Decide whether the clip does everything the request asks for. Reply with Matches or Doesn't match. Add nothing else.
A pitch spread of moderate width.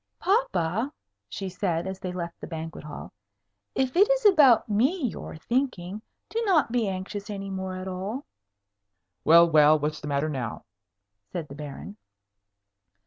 Doesn't match